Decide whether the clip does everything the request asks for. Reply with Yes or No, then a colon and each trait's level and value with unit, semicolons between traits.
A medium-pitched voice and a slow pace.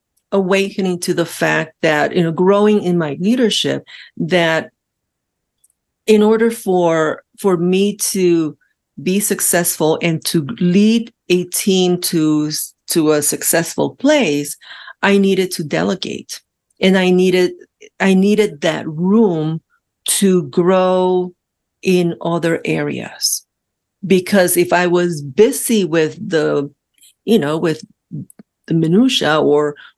Yes: medium, 180 Hz; slow, 120 wpm